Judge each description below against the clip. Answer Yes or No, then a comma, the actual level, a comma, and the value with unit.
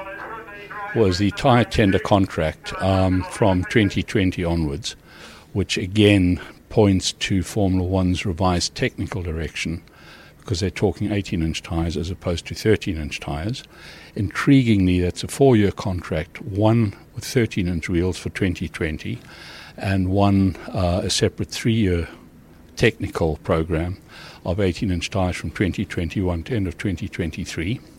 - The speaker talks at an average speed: No, slow, 120 wpm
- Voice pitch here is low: Yes, very low, 95 Hz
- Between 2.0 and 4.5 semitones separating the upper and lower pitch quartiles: Yes, average, 3.4 semitones